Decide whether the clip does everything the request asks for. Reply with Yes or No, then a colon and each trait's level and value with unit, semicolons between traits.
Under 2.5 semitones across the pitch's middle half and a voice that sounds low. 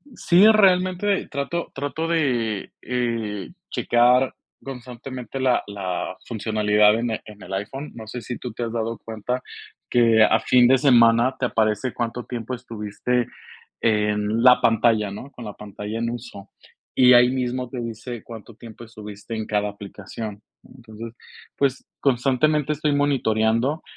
No: average, 2.9 semitones; low, 120 Hz